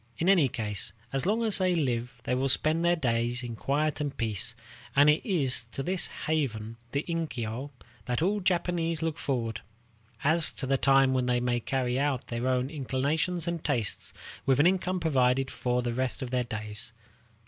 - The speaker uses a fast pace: No, average, 185 wpm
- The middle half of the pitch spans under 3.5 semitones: No, average, 4.7 semitones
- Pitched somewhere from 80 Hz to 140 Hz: Yes, low, 135 Hz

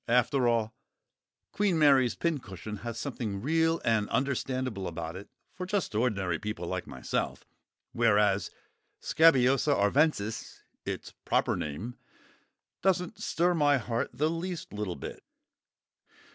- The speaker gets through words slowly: Yes, slow, 115 wpm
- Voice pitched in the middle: No, low, 120 Hz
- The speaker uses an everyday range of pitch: No, wide, 6.7 semitones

